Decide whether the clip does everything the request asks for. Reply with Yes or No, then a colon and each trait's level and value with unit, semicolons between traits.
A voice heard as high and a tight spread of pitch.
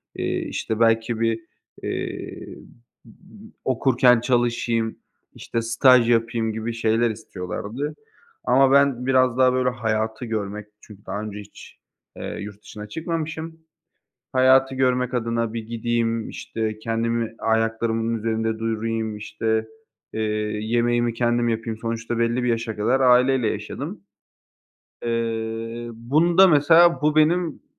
No: low, 115 Hz; narrow, 2.3 semitones